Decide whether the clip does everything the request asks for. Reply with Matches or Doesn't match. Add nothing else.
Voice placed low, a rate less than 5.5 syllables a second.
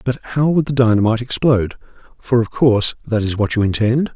Doesn't match